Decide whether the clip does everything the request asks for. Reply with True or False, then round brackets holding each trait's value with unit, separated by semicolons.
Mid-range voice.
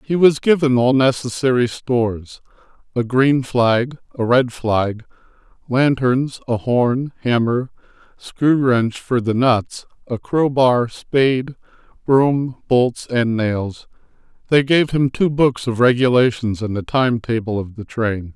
False (125 Hz)